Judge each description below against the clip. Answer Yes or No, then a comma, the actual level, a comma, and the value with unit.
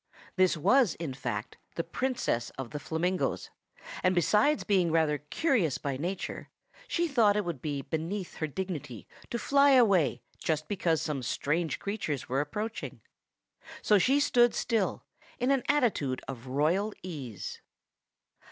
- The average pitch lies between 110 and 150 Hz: No, medium, 170 Hz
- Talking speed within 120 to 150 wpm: Yes, average, 145 wpm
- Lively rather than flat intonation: Yes, wide, 6.7 semitones